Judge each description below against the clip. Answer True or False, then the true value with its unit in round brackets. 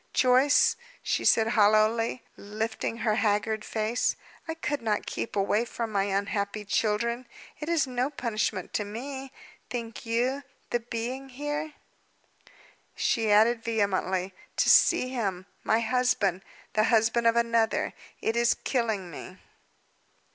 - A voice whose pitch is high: True (230 Hz)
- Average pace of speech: False (130 wpm)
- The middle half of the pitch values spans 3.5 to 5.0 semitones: False (2.8 semitones)